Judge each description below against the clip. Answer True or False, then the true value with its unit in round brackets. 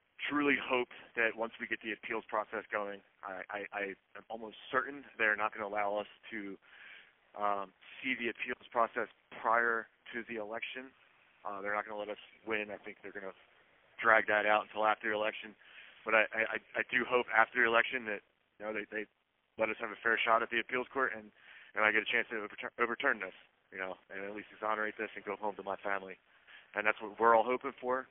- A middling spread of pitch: False (2.1 semitones)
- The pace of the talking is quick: True (220 wpm)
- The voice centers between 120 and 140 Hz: False (110 Hz)